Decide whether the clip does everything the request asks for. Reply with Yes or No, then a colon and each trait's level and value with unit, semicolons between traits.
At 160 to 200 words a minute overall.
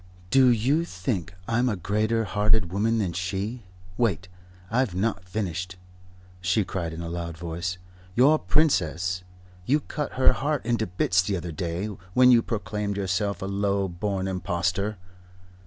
No: average, 150 wpm